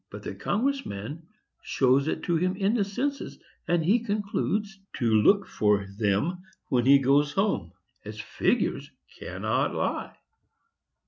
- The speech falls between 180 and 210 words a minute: No, average, 140 wpm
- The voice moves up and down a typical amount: No, wide, 7.6 semitones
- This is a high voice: No, medium, 175 Hz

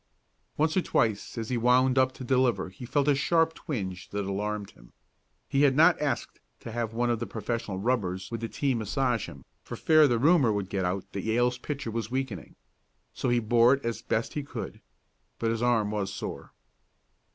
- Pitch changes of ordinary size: Yes, average, 3.9 semitones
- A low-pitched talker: Yes, low, 120 Hz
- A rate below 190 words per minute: No, average, 200 wpm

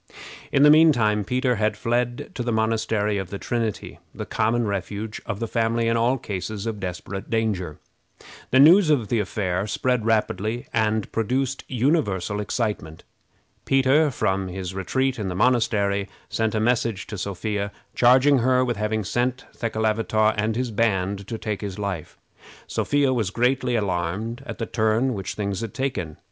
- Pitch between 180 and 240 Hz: No, low, 110 Hz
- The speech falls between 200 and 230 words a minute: No, average, 165 wpm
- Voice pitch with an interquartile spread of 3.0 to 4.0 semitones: Yes, average, 3.4 semitones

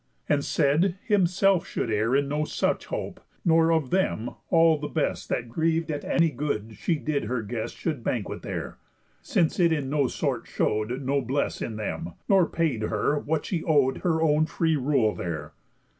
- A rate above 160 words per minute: Yes, average, 175 wpm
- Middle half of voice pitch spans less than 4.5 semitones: No, average, 5.1 semitones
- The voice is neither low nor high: Yes, medium, 145 Hz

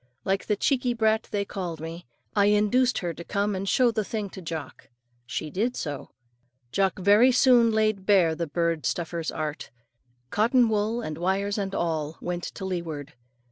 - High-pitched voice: Yes, high, 195 Hz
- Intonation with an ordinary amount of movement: Yes, average, 4.4 semitones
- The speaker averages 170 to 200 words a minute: Yes, average, 175 wpm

